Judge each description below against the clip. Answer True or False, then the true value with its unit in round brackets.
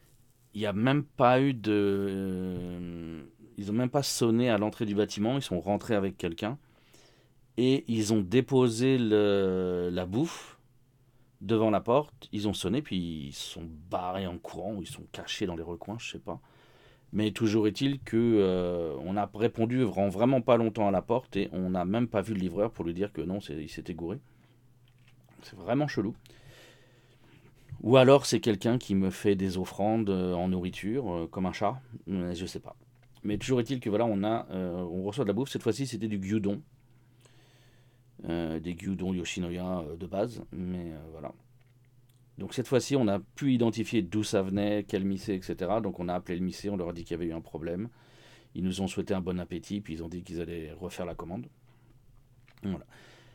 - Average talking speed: True (200 wpm)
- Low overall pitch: True (105 Hz)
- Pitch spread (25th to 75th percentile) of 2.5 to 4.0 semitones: False (5.1 semitones)